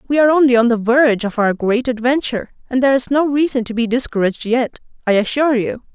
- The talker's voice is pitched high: Yes, high, 245 Hz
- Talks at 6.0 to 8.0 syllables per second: Yes, 6.4 syllables/s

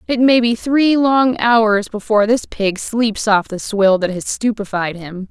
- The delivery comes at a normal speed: Yes, average, 180 wpm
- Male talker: No, female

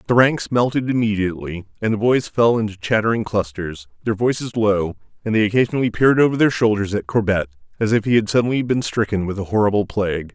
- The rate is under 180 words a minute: No, average, 195 wpm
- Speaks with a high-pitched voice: No, low, 105 Hz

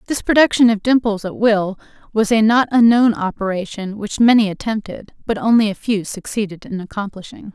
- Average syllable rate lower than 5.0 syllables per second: No, 5.4 syllables/s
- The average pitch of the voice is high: Yes, high, 215 Hz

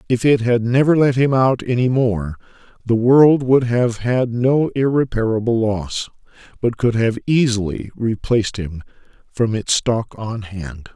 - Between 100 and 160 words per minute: Yes, average, 155 wpm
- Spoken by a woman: No, male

